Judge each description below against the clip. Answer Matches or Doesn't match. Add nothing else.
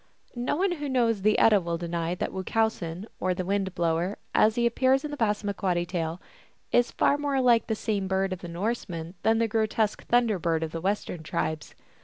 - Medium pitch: Doesn't match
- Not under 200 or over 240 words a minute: Matches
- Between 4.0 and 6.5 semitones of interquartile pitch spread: Matches